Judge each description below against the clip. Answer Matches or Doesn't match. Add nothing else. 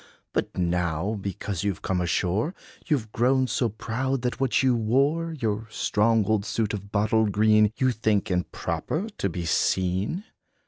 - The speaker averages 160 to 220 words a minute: Matches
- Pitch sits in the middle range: Doesn't match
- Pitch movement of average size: Matches